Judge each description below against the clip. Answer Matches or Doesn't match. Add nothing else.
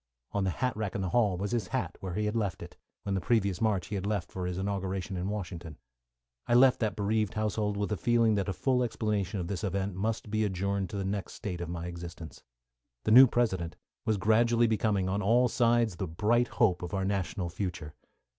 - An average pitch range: Matches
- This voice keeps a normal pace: Doesn't match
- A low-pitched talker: Matches